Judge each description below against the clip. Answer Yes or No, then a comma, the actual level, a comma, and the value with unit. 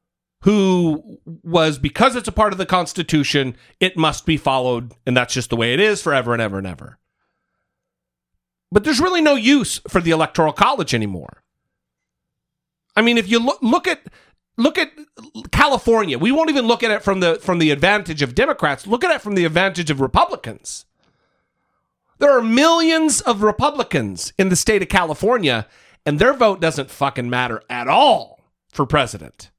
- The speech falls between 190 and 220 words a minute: No, average, 175 wpm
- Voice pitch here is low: No, medium, 185 Hz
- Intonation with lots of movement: Yes, wide, 8.8 semitones